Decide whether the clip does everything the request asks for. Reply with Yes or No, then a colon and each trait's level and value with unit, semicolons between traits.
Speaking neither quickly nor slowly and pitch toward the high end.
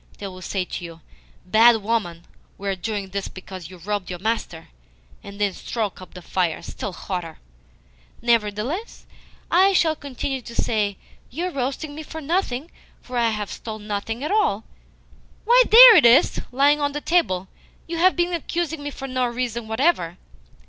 Yes: average, 175 wpm; high, 230 Hz